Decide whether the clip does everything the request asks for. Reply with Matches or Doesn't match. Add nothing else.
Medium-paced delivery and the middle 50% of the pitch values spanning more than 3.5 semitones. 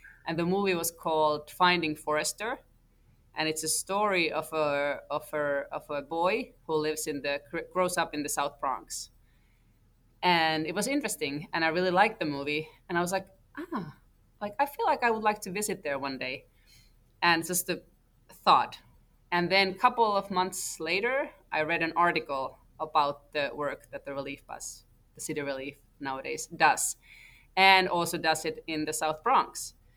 Matches